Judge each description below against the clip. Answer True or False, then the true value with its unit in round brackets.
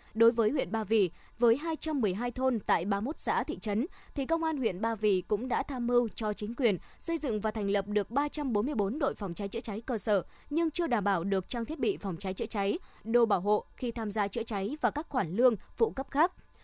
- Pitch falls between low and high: False (230 Hz)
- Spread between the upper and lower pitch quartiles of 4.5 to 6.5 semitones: False (4.0 semitones)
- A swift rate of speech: False (240 wpm)